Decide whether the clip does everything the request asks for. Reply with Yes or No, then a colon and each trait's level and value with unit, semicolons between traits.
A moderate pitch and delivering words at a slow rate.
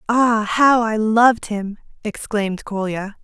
No: high, 220 Hz; slow, 130 wpm